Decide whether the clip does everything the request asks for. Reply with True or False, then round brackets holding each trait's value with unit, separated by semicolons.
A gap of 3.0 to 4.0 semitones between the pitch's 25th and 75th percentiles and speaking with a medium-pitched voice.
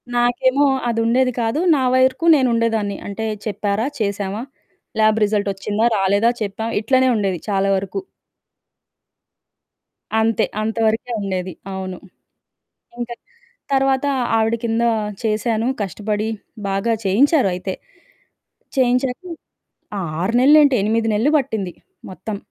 False (3.5 semitones; 225 Hz)